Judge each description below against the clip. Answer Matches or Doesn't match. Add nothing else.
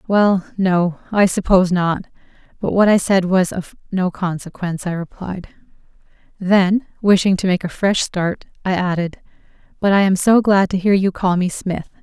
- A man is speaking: Doesn't match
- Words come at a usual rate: Matches